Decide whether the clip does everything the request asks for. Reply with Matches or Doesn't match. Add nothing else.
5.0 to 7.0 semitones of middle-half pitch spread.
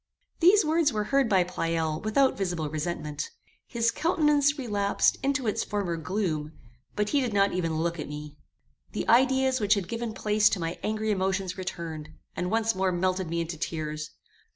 Matches